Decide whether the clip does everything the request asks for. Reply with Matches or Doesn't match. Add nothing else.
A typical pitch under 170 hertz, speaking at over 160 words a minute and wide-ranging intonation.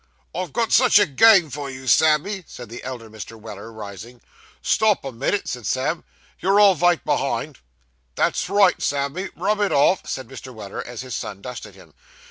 Matches